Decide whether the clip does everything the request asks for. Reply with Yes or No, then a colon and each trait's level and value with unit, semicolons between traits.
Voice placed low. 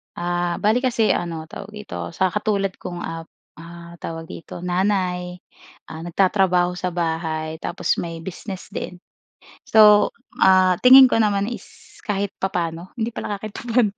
No: medium, 185 Hz